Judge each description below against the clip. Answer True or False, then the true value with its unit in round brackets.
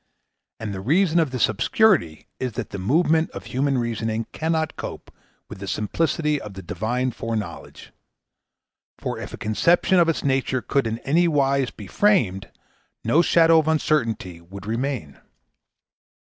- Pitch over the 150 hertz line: False (130 Hz)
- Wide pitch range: True (6.8 semitones)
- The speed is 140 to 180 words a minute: True (150 wpm)